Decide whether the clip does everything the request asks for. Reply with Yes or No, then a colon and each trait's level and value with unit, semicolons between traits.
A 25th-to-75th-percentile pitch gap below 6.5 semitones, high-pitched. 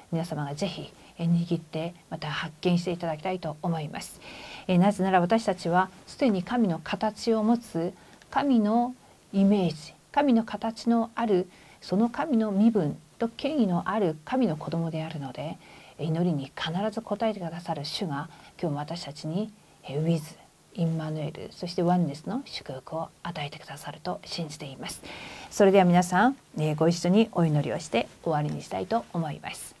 No: average, 5.3 semitones; medium, 180 Hz